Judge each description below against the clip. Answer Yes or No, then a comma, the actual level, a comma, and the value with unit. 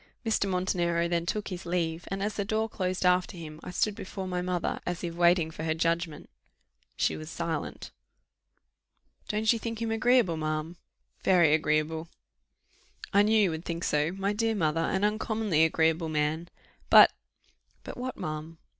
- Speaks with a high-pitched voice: No, medium, 175 Hz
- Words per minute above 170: No, average, 165 wpm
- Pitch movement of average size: Yes, average, 4.0 semitones